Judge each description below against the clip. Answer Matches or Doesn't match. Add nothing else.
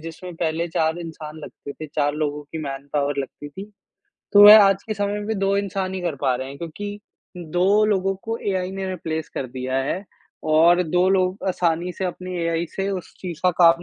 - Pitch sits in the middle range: Matches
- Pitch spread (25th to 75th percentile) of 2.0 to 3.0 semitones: Doesn't match